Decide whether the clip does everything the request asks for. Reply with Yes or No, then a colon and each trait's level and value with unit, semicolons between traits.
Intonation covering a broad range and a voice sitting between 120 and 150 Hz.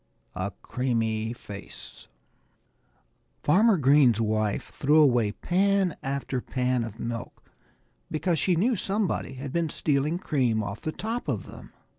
Yes: wide, 6.8 semitones; low, 135 Hz